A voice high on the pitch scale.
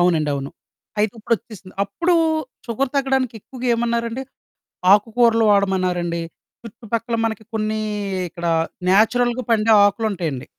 Yes: high, 220 Hz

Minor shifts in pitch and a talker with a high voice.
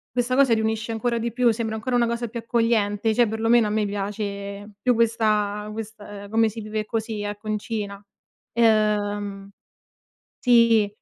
Yes: narrow, 2.0 semitones; high, 220 Hz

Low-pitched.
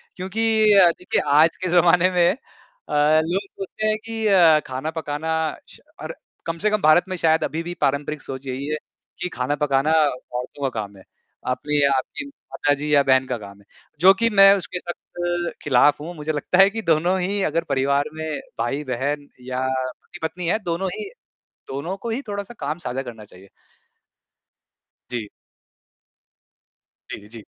No: medium, 155 Hz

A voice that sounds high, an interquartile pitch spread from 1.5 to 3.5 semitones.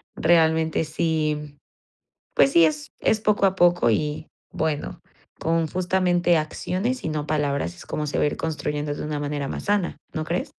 No: medium, 160 Hz; average, 2.8 semitones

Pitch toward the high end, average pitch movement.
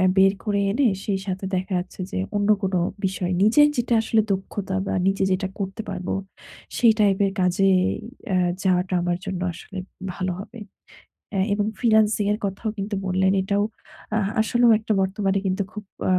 No: high, 195 Hz; narrow, 1.9 semitones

